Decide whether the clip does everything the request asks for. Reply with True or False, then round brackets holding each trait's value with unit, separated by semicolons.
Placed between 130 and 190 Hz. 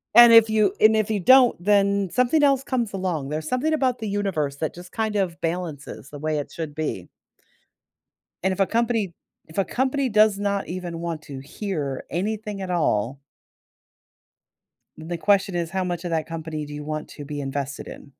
True (185 Hz)